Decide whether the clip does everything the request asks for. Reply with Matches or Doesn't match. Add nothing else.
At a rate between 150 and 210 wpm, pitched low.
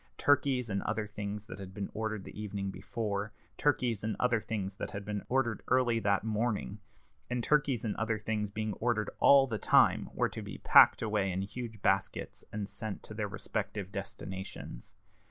Matches